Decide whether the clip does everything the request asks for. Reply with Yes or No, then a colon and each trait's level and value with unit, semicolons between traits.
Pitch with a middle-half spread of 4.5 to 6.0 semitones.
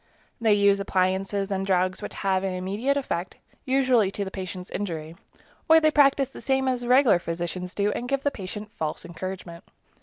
Yes: wide, 5.4 semitones